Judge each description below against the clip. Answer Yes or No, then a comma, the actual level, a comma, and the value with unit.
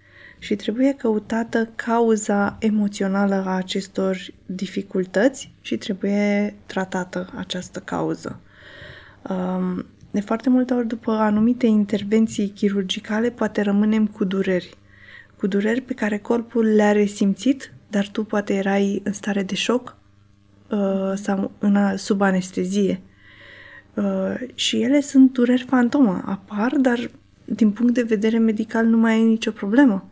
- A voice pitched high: Yes, high, 210 Hz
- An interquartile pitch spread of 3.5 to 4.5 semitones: No, average, 2.7 semitones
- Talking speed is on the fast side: No, average, 120 wpm